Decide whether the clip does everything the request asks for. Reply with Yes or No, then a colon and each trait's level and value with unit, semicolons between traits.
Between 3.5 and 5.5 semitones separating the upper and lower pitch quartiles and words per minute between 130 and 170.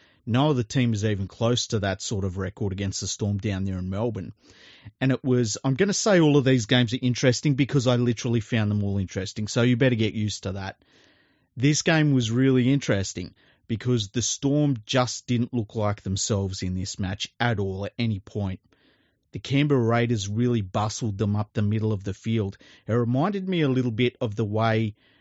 No: average, 3.8 semitones; fast, 205 wpm